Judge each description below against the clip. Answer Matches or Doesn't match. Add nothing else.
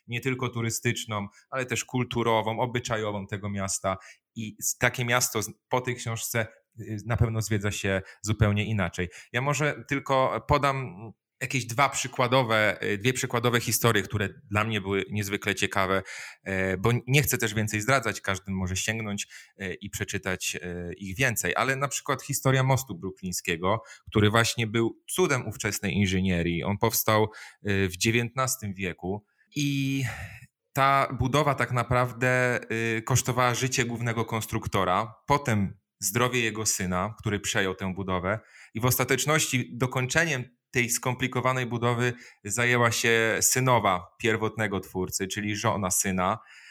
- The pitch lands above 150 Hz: Doesn't match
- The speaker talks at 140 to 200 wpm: Doesn't match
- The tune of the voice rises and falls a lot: Doesn't match